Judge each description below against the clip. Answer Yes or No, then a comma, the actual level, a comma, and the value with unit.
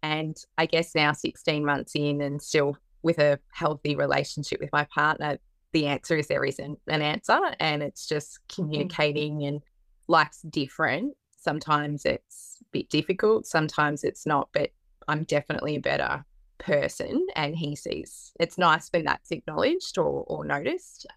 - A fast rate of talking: No, average, 155 wpm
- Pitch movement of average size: No, narrow, 1.9 semitones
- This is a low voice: No, medium, 150 Hz